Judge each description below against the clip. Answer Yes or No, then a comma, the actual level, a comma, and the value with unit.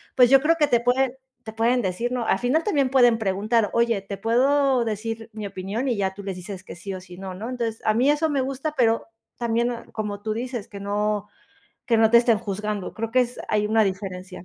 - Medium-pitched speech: No, high, 225 Hz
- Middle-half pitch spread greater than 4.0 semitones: No, average, 3.4 semitones